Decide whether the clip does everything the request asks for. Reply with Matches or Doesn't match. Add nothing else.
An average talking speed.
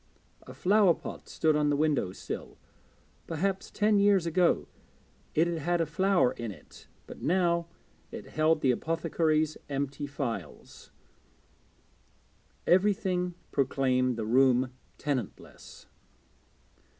Doesn't match